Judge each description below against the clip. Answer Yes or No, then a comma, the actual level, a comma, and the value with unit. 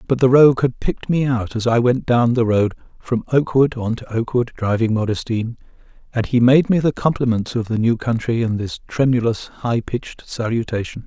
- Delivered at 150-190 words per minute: No, fast, 205 wpm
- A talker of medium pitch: No, low, 120 Hz